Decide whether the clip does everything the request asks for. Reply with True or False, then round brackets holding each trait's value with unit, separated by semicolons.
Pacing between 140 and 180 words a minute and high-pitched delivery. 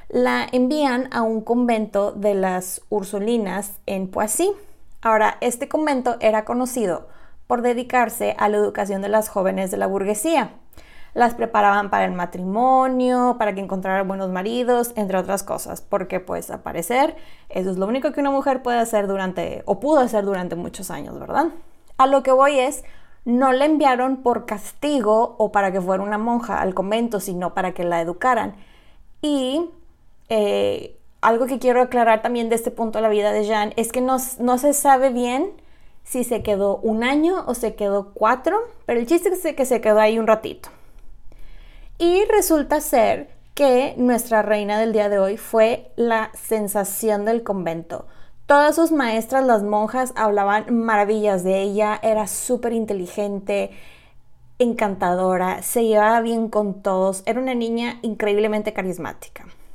True (165 wpm; 220 Hz)